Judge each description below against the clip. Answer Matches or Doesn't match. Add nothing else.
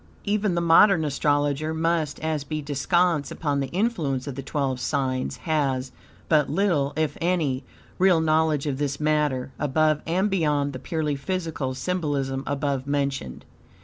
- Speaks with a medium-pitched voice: Matches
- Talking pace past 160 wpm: Doesn't match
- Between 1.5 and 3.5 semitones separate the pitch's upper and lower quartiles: Matches